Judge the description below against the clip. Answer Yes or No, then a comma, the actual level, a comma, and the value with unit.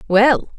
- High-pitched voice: Yes, high, 230 Hz